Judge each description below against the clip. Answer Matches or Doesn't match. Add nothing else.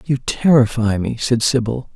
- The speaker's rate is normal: Matches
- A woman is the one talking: Doesn't match